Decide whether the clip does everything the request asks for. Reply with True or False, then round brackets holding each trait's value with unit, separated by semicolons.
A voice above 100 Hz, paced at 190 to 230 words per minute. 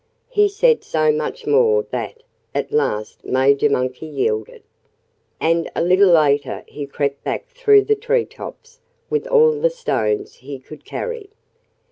False (185 Hz; 145 wpm)